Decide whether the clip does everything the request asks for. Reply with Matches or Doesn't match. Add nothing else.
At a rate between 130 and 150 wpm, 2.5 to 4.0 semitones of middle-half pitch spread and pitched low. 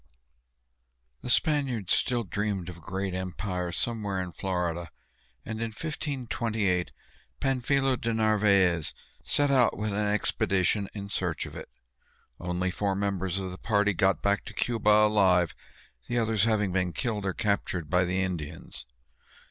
Matches